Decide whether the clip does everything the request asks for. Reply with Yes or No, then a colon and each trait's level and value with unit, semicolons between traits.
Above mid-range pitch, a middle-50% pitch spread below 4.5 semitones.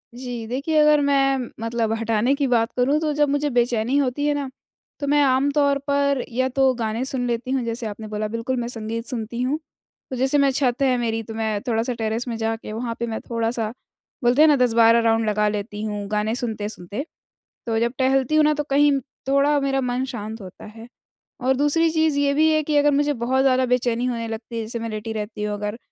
Yes: high, 245 Hz; average, 3.6 semitones